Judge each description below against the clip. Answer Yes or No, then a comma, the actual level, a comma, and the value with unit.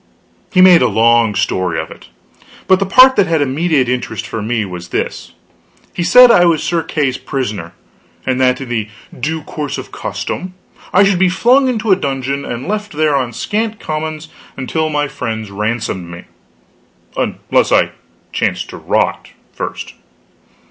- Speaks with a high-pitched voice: No, medium, 145 Hz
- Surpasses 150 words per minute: Yes, average, 165 wpm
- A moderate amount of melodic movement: No, wide, 7.5 semitones